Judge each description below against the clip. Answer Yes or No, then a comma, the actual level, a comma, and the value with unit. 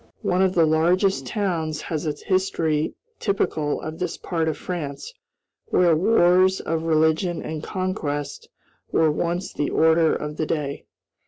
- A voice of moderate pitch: Yes, medium, 165 Hz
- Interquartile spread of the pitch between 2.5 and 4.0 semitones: Yes, average, 2.8 semitones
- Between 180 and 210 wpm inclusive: No, average, 145 wpm